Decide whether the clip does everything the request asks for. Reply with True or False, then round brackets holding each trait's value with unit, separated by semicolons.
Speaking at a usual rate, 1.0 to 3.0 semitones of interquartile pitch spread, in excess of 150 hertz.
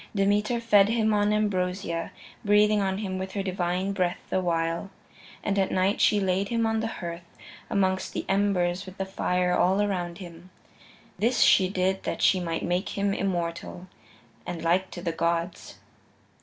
True (170 wpm; 2.4 semitones; 190 Hz)